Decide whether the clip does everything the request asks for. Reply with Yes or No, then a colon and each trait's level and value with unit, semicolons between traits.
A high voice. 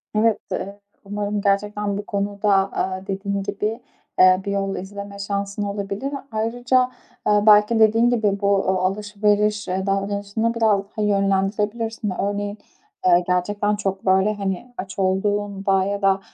Yes: high, 200 Hz